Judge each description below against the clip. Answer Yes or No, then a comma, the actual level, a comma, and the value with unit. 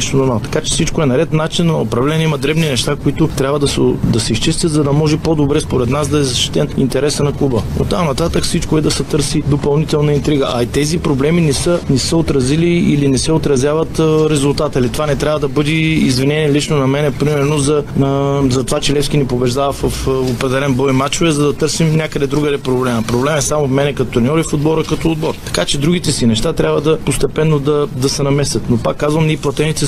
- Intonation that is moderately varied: No, narrow, 2.1 semitones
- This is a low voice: No, medium, 145 Hz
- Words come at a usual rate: No, fast, 230 wpm